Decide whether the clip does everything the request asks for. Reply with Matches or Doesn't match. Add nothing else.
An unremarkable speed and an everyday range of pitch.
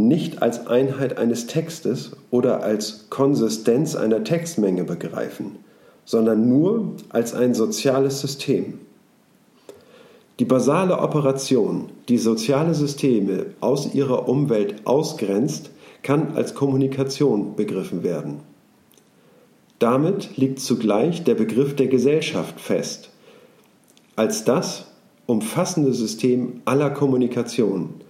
Doesn't match